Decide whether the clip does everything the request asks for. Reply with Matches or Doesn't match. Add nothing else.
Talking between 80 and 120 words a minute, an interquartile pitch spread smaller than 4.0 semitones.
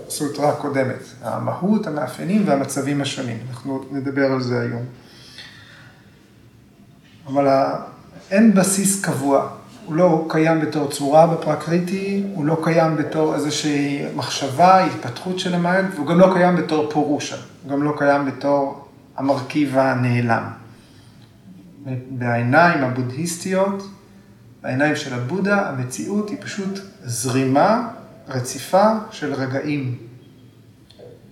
Doesn't match